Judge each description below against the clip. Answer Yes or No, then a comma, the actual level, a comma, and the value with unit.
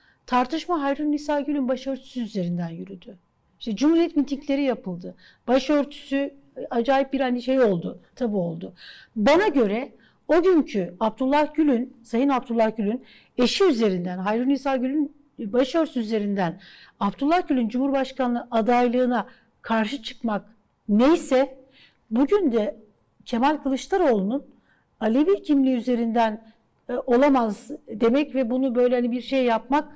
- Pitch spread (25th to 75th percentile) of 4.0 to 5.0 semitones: No, average, 3.6 semitones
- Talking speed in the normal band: Yes, average, 120 wpm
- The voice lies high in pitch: Yes, very high, 255 Hz